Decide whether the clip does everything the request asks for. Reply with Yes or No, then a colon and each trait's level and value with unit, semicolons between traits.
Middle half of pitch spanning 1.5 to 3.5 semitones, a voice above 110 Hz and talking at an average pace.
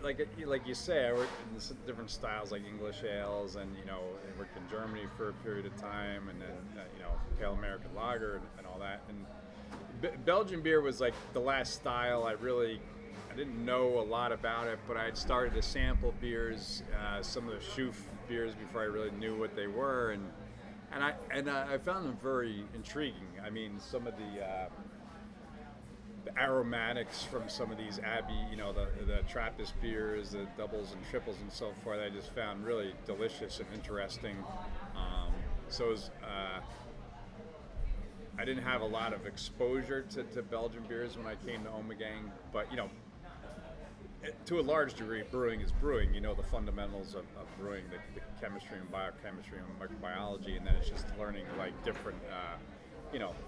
No: average, 3.2 semitones; low, 105 Hz; average, 190 wpm